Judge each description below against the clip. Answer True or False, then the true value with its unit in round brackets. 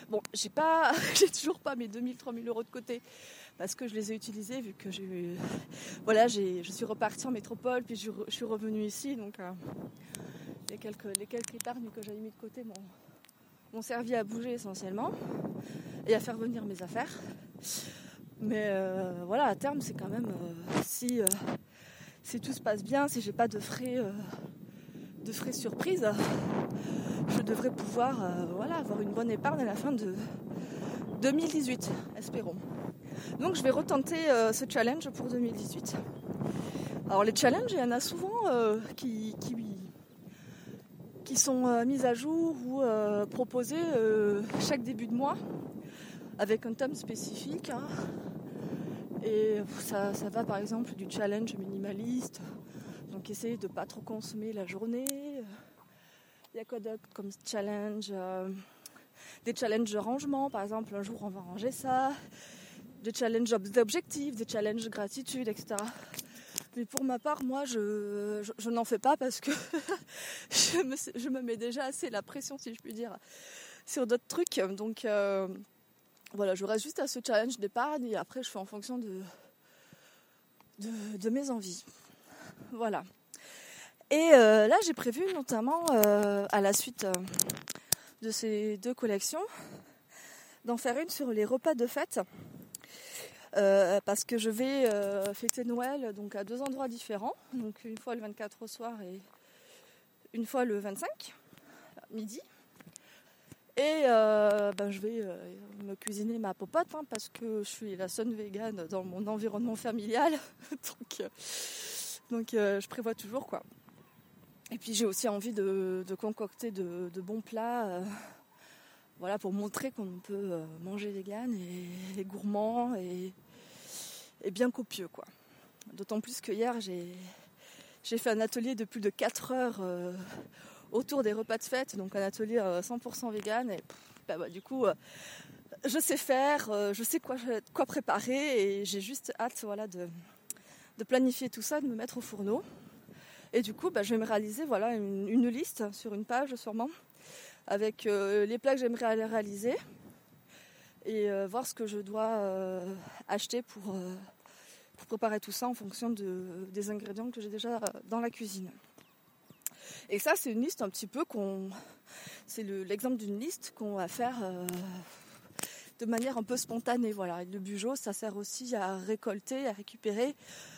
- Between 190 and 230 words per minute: False (170 wpm)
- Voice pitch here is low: False (220 Hz)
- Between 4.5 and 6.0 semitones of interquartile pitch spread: False (3.5 semitones)